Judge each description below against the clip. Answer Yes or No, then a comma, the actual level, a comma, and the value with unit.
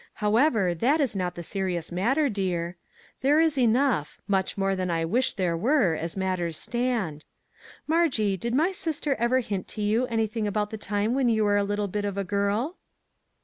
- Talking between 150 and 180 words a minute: No, average, 190 wpm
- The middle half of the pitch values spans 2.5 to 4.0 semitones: No, average, 5.0 semitones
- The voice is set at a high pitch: Yes, high, 210 Hz